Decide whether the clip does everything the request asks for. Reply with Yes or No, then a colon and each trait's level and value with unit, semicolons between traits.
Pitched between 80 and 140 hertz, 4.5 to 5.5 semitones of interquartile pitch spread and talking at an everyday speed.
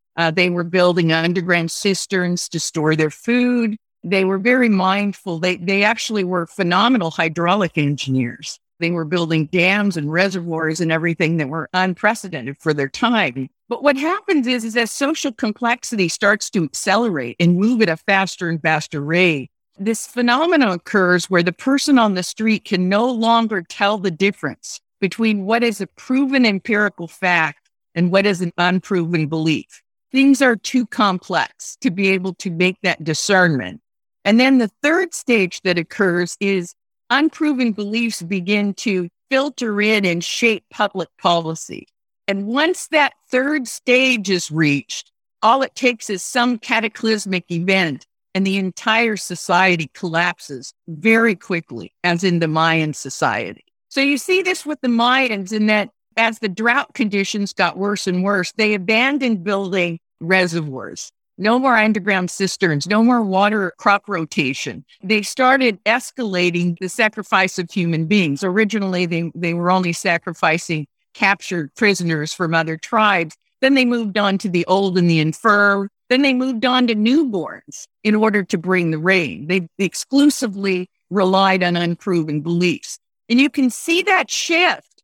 No: high, 195 Hz; average, 4.8 semitones; average, 155 wpm